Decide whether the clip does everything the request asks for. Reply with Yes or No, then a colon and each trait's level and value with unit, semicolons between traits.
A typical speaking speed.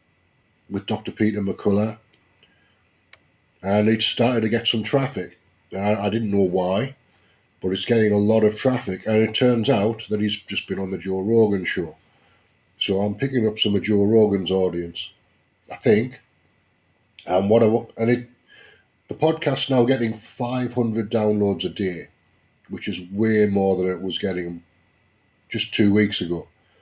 Yes: average, 160 wpm